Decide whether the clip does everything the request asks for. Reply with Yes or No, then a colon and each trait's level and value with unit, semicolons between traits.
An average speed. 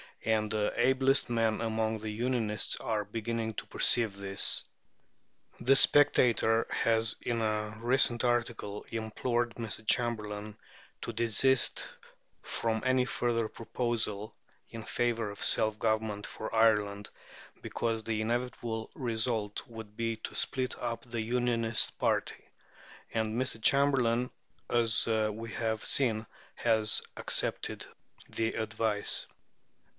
No: slow, 115 wpm